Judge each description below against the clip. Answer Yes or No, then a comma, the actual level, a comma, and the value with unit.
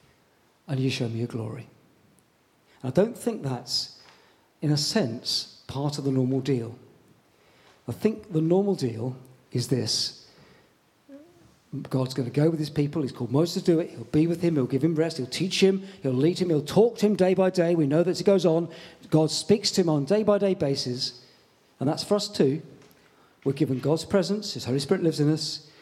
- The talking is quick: Yes, fast, 215 wpm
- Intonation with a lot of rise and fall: Yes, wide, 5.8 semitones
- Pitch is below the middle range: No, medium, 155 Hz